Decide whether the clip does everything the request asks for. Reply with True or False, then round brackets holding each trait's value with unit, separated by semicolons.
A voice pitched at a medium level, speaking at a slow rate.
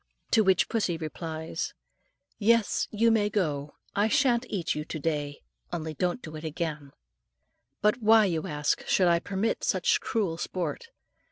False (180 Hz; 155 wpm)